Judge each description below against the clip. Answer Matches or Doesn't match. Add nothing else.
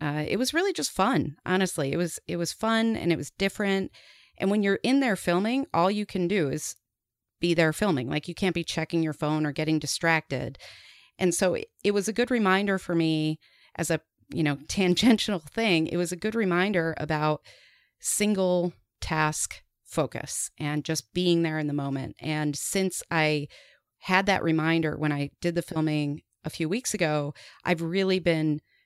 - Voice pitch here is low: Doesn't match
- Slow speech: Doesn't match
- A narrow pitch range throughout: Doesn't match